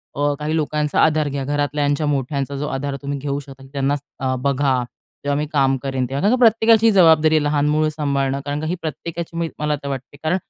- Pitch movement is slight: Yes, narrow, 2.1 semitones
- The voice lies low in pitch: No, medium, 145 Hz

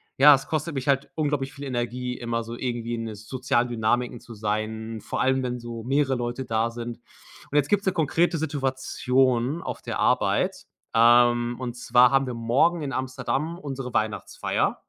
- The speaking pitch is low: Yes, low, 125 Hz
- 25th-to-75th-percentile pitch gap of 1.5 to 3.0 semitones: Yes, narrow, 2.6 semitones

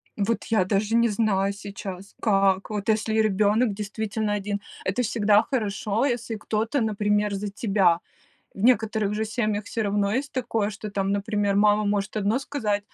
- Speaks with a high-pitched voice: Yes, high, 210 Hz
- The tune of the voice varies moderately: No, narrow, 1.6 semitones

